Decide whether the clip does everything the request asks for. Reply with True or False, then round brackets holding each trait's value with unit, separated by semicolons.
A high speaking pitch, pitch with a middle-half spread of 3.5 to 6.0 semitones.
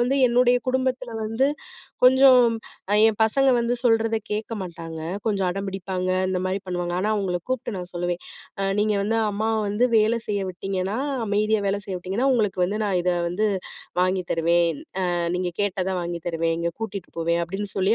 True (200 Hz; 3.8 semitones)